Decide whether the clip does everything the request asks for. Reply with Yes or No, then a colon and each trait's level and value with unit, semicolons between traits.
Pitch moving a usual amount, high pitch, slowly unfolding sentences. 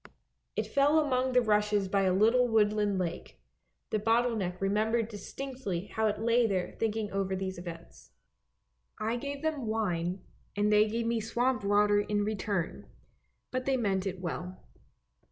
No: average, 3.3 semitones; high, 210 Hz; average, 160 wpm